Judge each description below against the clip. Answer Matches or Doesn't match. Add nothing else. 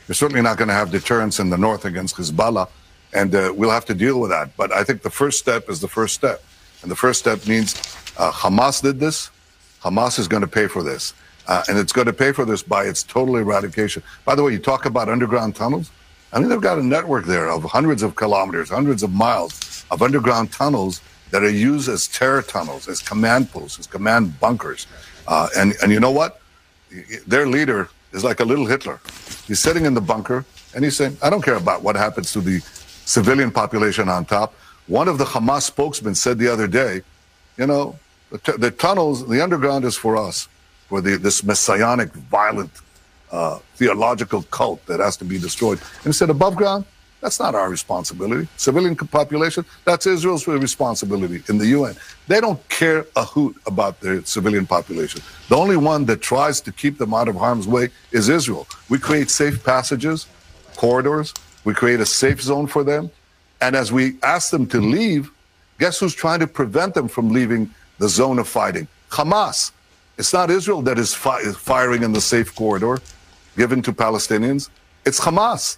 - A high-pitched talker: Doesn't match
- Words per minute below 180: Doesn't match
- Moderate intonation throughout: Doesn't match